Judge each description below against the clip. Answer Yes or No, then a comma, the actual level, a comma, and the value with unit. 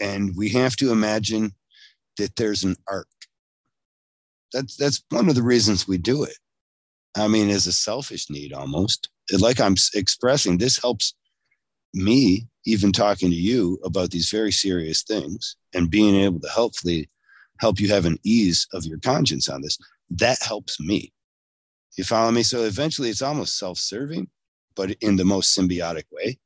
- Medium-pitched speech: No, low, 100 Hz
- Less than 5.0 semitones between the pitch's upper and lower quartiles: Yes, average, 3.7 semitones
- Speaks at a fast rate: No, average, 165 wpm